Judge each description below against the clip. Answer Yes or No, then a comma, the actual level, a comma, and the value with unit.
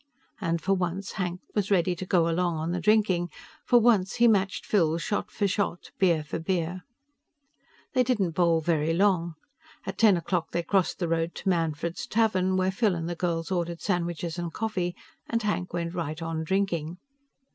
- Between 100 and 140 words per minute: No, average, 180 wpm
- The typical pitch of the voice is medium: Yes, medium, 175 Hz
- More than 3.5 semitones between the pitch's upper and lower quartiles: No, average, 2.7 semitones